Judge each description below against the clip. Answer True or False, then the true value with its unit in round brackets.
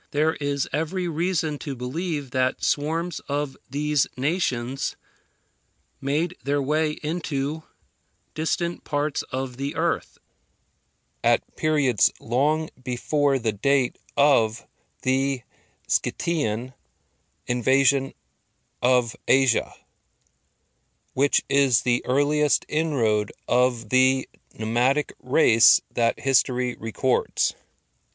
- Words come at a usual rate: False (95 wpm)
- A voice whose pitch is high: False (135 Hz)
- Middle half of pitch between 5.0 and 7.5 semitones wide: False (3.1 semitones)